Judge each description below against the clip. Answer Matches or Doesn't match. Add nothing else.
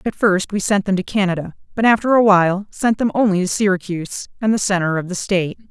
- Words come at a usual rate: Doesn't match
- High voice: Matches